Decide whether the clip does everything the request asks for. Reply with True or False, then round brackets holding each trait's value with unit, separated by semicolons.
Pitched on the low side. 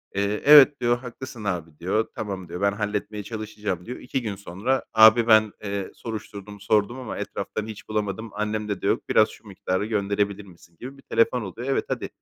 True (105 Hz)